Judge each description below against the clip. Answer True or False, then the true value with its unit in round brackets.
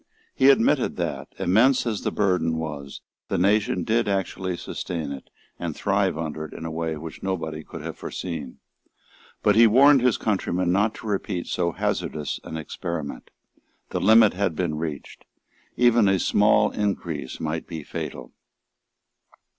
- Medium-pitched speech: False (90 Hz)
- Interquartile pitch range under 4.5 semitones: False (4.8 semitones)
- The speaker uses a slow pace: False (155 wpm)